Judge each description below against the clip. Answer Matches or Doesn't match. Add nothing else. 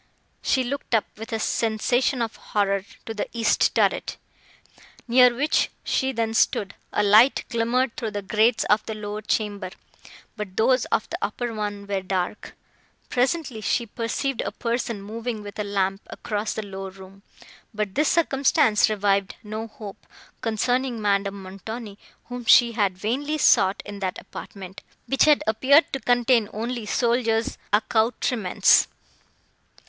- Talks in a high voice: Matches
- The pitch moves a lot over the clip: Doesn't match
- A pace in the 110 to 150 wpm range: Matches